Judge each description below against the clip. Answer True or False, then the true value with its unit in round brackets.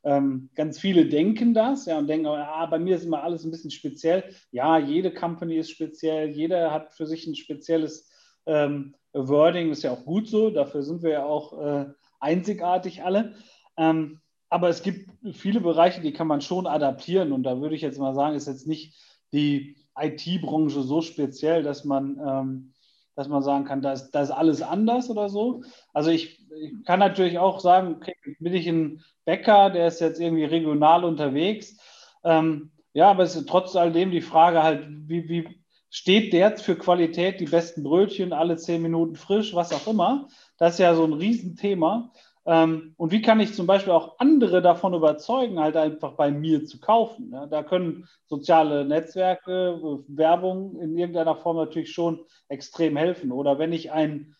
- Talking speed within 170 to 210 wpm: True (185 wpm)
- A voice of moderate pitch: True (165 Hz)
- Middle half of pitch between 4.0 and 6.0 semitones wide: False (3.1 semitones)